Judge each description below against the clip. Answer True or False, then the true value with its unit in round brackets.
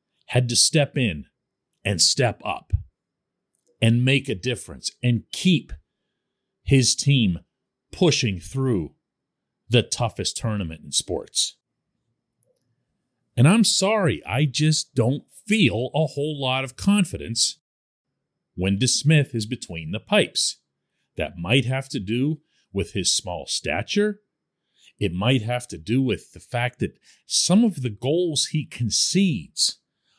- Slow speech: True (125 wpm)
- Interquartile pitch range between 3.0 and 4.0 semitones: False (5.0 semitones)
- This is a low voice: True (130 Hz)